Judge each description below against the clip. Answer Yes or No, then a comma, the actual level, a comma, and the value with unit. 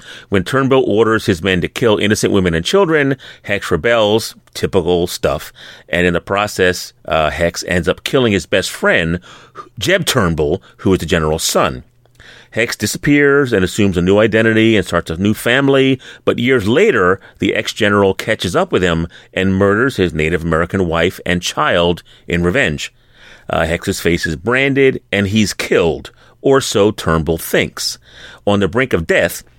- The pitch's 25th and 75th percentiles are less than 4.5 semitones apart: No, average, 5.3 semitones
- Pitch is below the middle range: Yes, low, 100 Hz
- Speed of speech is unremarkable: Yes, average, 170 wpm